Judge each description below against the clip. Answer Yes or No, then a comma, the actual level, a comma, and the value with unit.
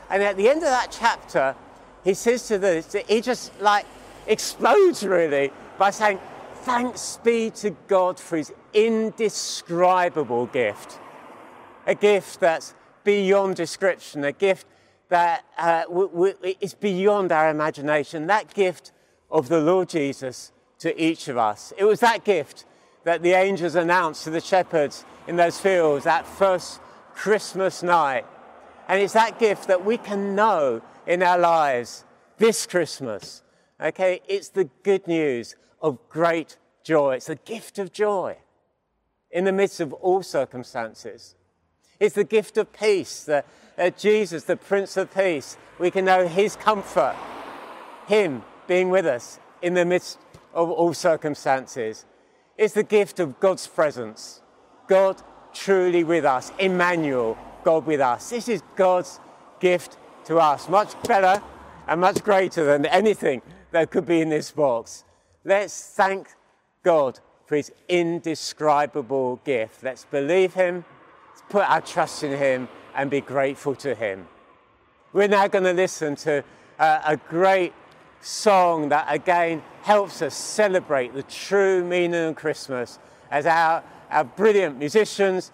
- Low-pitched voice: No, medium, 180 Hz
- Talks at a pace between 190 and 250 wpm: No, average, 145 wpm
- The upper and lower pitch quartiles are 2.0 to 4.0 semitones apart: No, average, 4.4 semitones